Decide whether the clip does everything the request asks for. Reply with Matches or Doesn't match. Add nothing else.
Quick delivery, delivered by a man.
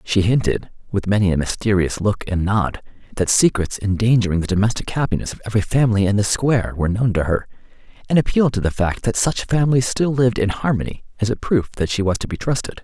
Matches